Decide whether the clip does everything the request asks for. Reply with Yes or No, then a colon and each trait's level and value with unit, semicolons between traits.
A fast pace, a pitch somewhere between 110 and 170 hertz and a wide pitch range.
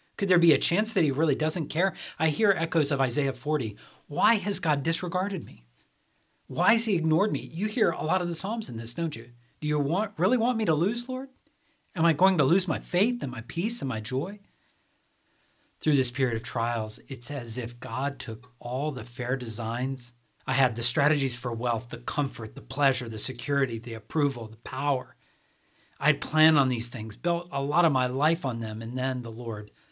Yes: fast, 215 wpm; medium, 140 Hz; wide, 5.9 semitones